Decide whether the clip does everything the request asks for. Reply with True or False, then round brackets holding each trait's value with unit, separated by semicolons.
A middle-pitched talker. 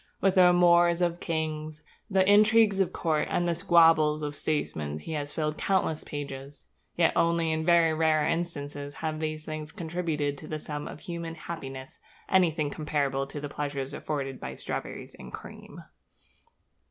True (155 Hz)